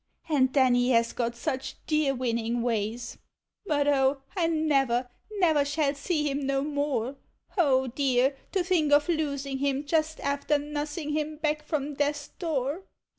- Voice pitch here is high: Yes, very high, 285 Hz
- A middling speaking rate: Yes, average, 160 wpm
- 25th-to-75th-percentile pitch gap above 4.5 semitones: No, narrow, 2.6 semitones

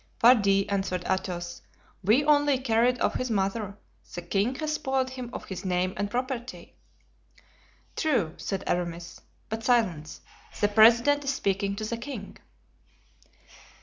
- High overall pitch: Yes, high, 220 Hz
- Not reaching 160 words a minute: Yes, slow, 135 wpm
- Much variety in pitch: No, average, 5.0 semitones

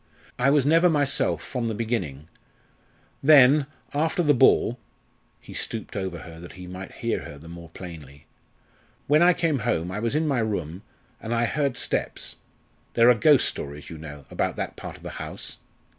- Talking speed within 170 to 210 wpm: Yes, average, 180 wpm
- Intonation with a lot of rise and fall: Yes, wide, 8.8 semitones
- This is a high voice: No, low, 115 Hz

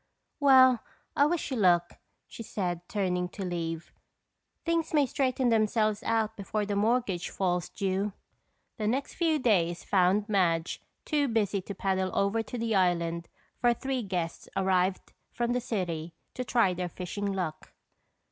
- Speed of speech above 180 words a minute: No, average, 150 wpm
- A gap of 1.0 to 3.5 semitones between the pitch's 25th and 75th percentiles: No, average, 4.9 semitones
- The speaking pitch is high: Yes, high, 200 Hz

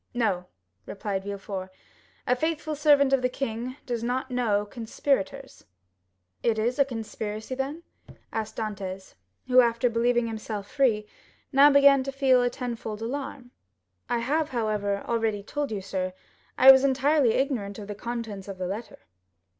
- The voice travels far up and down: No, average, 4.2 semitones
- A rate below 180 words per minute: Yes, average, 155 wpm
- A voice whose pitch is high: Yes, high, 235 Hz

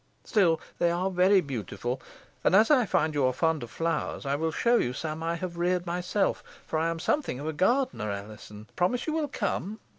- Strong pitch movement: No, average, 5.0 semitones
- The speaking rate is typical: No, fast, 210 wpm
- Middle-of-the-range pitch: Yes, medium, 165 Hz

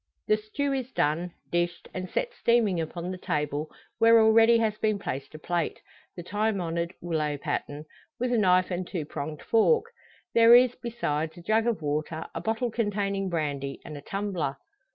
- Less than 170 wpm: No, average, 175 wpm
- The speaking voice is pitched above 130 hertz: Yes, medium, 185 Hz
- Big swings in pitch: Yes, wide, 6.1 semitones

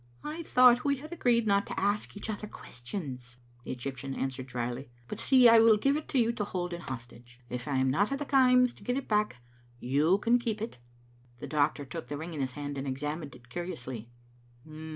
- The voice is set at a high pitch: No, medium, 160 Hz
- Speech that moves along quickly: Yes, fast, 235 wpm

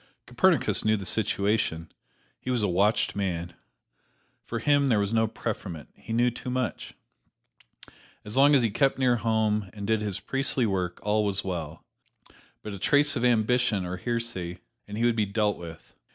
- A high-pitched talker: No, low, 110 Hz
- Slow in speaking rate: No, average, 175 wpm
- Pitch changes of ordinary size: Yes, average, 3.6 semitones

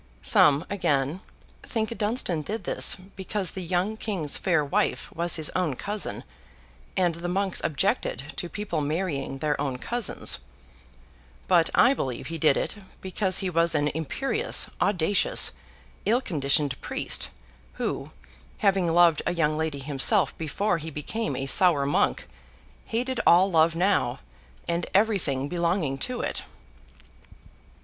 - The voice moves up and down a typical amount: Yes, average, 4.9 semitones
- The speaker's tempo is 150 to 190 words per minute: No, slow, 135 wpm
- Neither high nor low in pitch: Yes, medium, 170 Hz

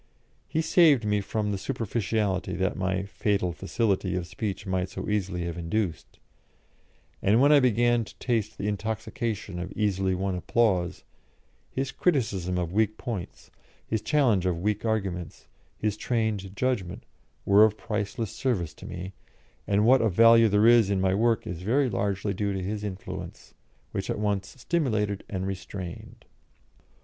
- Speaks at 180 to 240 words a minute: No, average, 155 wpm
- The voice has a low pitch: Yes, low, 105 Hz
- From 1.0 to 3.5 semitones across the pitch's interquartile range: Yes, average, 3.2 semitones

